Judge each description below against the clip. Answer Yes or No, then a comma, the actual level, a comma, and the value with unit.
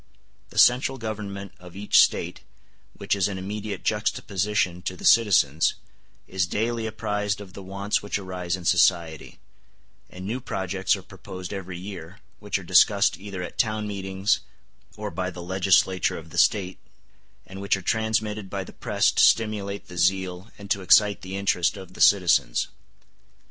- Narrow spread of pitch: Yes, narrow, 2.2 semitones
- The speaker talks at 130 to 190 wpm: Yes, average, 165 wpm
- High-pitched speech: No, very low, 95 Hz